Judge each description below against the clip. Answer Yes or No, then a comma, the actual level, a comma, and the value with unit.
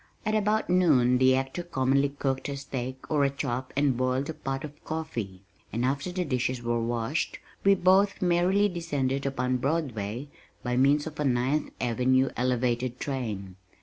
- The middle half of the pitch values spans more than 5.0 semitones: No, average, 3.6 semitones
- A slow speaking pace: No, average, 165 wpm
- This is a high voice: No, low, 135 Hz